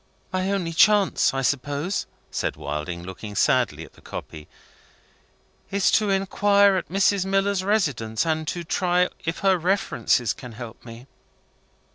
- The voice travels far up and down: Yes, wide, 8.2 semitones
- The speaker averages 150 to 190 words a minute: No, average, 140 wpm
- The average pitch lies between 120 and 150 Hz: No, medium, 175 Hz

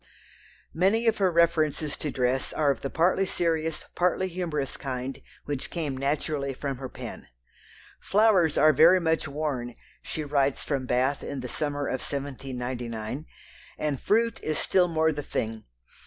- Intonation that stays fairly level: No, average, 3.8 semitones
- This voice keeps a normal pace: Yes, average, 155 wpm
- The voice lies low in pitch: No, medium, 150 Hz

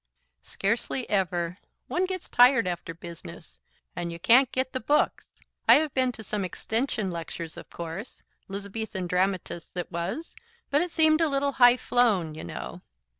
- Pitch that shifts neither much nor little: No, wide, 6.9 semitones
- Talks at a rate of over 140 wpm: Yes, average, 160 wpm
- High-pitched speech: Yes, high, 210 Hz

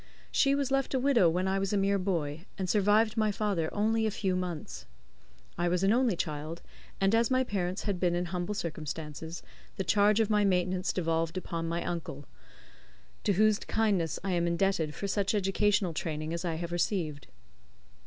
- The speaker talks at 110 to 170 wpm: No, average, 185 wpm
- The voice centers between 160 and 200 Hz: Yes, medium, 185 Hz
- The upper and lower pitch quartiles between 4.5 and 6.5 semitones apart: No, average, 3.6 semitones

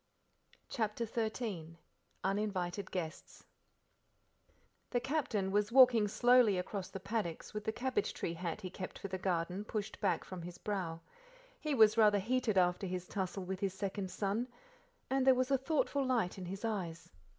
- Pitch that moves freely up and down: No, average, 3.8 semitones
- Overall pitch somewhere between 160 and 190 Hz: No, high, 200 Hz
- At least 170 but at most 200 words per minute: No, average, 160 wpm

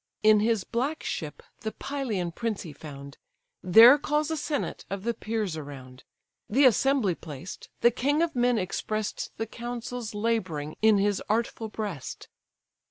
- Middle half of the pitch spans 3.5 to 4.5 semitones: No, average, 5.1 semitones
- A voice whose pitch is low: No, high, 220 Hz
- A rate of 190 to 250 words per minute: No, average, 150 wpm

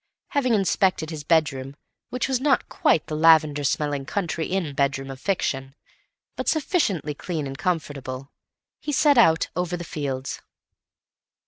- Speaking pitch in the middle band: Yes, medium, 160 Hz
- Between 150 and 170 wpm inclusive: No, average, 140 wpm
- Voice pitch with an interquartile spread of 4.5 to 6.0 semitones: Yes, wide, 5.5 semitones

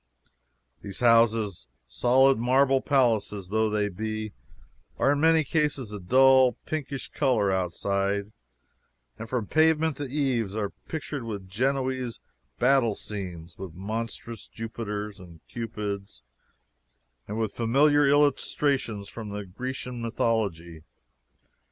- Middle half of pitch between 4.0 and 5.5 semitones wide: Yes, average, 4.7 semitones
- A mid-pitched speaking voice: No, low, 115 Hz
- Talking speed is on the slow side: Yes, slow, 115 wpm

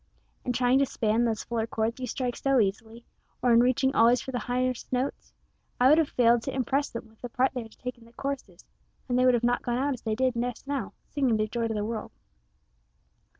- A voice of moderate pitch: No, high, 245 Hz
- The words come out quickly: Yes, fast, 240 wpm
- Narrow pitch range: Yes, narrow, 2.0 semitones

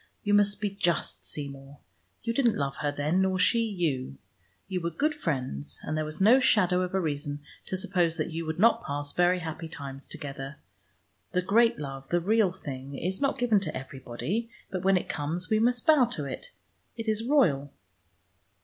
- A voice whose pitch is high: No, medium, 175 Hz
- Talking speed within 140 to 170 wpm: No, average, 190 wpm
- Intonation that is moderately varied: No, wide, 6.4 semitones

